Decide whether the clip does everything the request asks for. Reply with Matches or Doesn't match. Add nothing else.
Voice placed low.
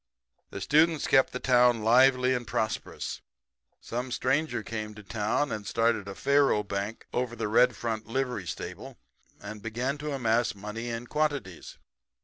Matches